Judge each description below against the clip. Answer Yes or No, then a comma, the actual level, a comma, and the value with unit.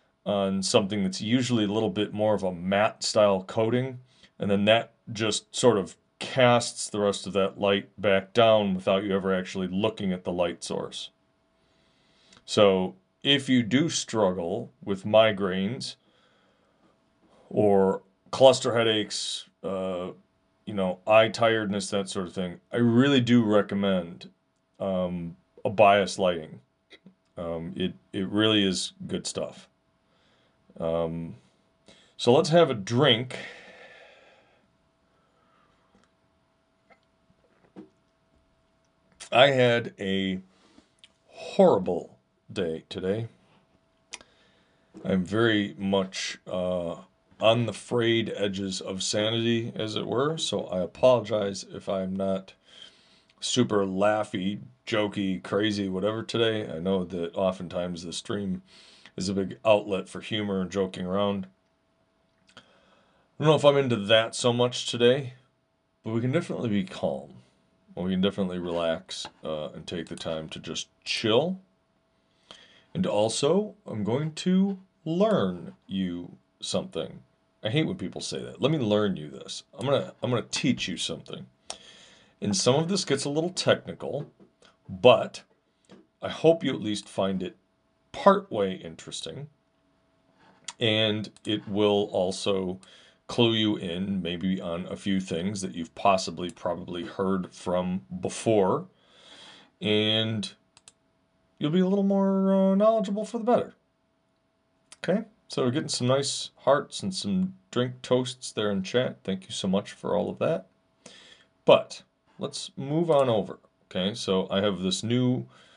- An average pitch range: Yes, average, 4.3 semitones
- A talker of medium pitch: No, low, 100 Hz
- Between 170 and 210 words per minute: No, slow, 135 wpm